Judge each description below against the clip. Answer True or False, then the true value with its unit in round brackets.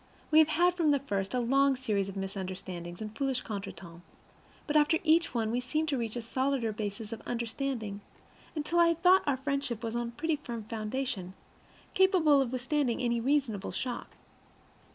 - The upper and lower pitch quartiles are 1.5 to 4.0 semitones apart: False (5.3 semitones)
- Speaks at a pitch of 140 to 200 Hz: False (250 Hz)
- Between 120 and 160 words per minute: False (180 wpm)